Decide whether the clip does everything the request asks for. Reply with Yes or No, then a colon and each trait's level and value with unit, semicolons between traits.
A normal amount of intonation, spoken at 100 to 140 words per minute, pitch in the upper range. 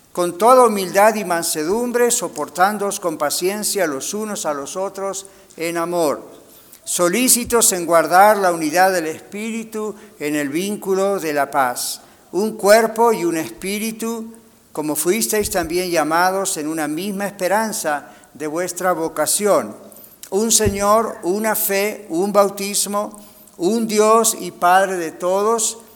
Yes: average, 3.7 semitones; average, 130 wpm; high, 195 Hz